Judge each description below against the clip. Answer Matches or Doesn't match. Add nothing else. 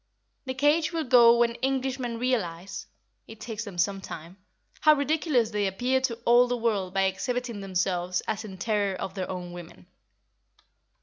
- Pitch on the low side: Doesn't match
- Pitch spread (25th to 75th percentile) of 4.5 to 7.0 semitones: Matches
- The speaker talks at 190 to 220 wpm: Doesn't match